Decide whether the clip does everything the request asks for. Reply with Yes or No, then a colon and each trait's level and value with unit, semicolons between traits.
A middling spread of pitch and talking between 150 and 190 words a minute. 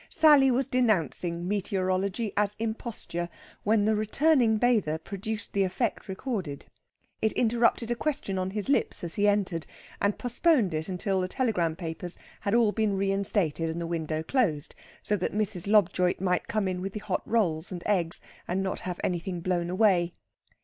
Yes: average, 3.8 semitones; average, 170 wpm